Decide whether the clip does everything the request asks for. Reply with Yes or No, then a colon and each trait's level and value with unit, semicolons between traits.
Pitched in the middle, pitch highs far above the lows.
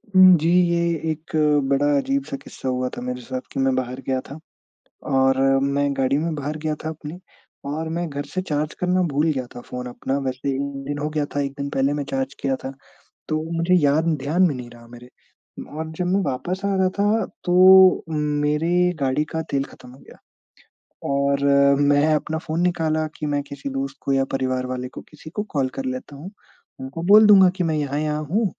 No: medium, 145 Hz; average, 3.4 semitones